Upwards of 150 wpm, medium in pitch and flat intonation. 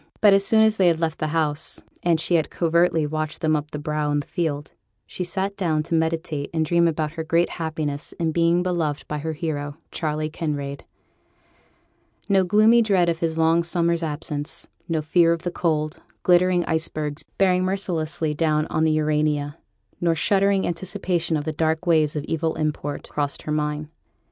Yes: average, 185 wpm; medium, 160 Hz; narrow, 2.3 semitones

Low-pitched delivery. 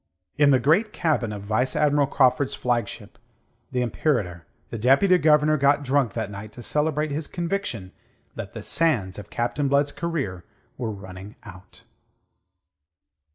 Yes: low, 130 Hz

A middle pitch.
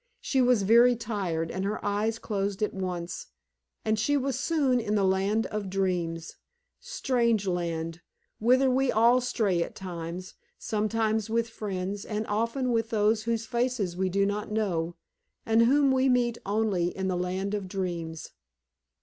No: high, 210 Hz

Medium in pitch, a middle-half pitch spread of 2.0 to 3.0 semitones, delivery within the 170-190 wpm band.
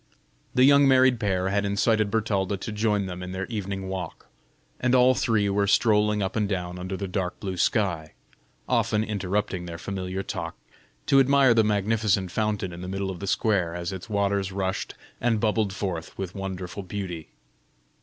No: low, 100 Hz; narrow, 2.5 semitones; average, 175 wpm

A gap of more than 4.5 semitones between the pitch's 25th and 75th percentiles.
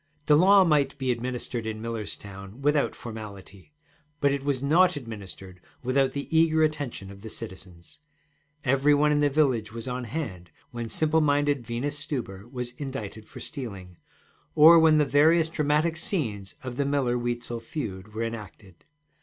Yes: average, 5.1 semitones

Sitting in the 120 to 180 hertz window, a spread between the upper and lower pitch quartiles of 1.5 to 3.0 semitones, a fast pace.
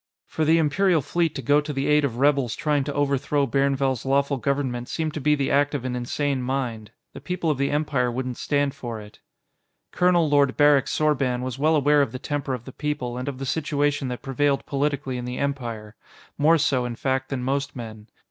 Yes: medium, 140 Hz; narrow, 2.5 semitones; fast, 215 wpm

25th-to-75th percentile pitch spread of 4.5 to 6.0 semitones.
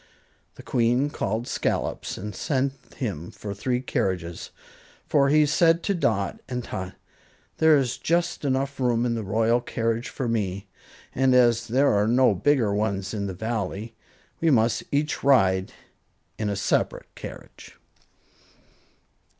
Yes: average, 4.9 semitones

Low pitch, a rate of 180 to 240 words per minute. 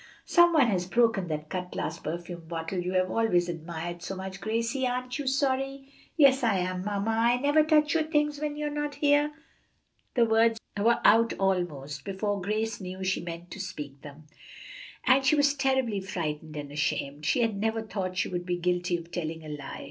No: high, 195 Hz; average, 195 wpm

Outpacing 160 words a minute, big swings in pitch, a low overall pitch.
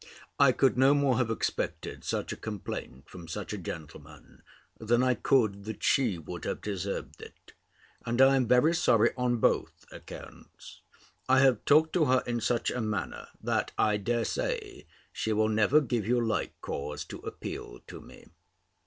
No: average, 170 wpm; average, 4.1 semitones; low, 115 Hz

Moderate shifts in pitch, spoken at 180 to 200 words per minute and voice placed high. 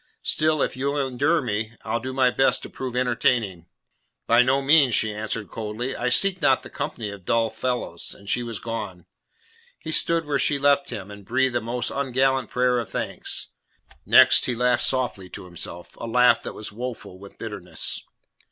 No: average, 3.4 semitones; average, 190 wpm; low, 125 Hz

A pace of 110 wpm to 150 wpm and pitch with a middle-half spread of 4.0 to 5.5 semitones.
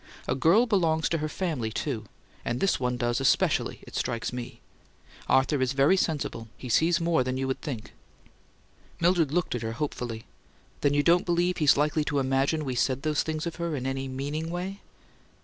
No: average, 185 wpm; average, 4.3 semitones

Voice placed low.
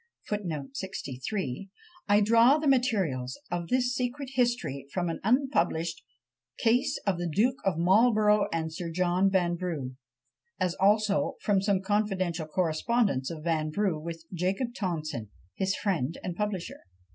No: high, 190 Hz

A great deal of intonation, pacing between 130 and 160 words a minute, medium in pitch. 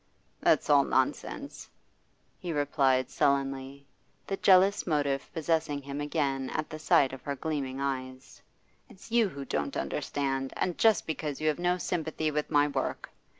No: average, 2.8 semitones; average, 150 wpm; medium, 145 Hz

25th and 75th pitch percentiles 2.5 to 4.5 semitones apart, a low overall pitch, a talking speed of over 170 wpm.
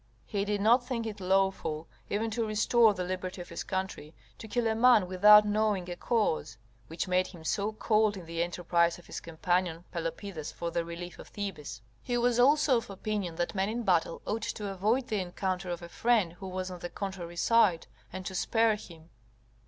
No: average, 3.8 semitones; high, 190 Hz; average, 200 wpm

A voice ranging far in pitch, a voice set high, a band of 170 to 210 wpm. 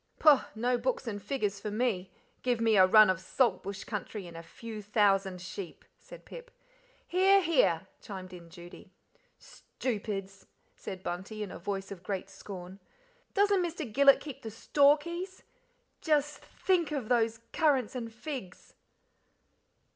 No: wide, 6.4 semitones; high, 220 Hz; average, 145 wpm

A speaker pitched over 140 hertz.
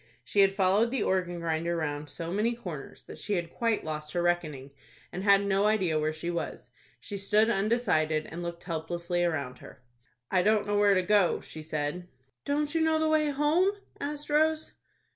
Yes: medium, 185 Hz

